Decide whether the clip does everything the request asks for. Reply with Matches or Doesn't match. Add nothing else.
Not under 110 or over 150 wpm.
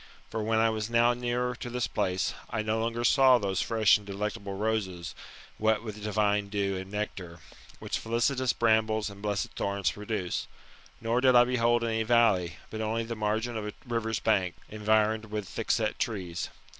Doesn't match